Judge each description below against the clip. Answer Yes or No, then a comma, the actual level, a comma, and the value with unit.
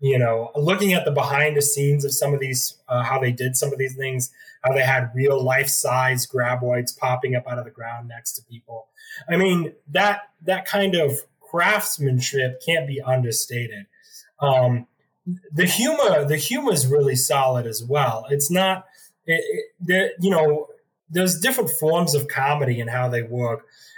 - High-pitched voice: No, medium, 140 Hz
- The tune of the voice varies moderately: No, wide, 6.0 semitones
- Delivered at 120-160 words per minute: No, average, 180 wpm